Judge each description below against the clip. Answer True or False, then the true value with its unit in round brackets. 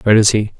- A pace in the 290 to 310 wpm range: True (300 wpm)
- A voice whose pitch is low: True (105 Hz)